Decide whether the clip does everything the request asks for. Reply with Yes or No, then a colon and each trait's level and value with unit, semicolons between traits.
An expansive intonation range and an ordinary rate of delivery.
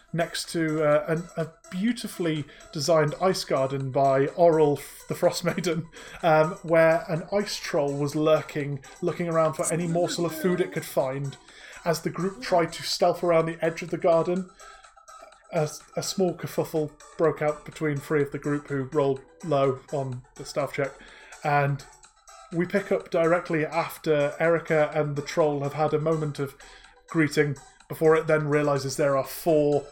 No: average, 2.7 semitones; average, 170 wpm